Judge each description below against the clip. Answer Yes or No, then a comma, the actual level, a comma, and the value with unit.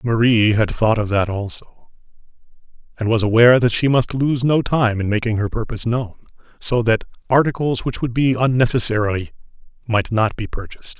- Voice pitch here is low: Yes, low, 115 Hz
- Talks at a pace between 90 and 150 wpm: No, average, 170 wpm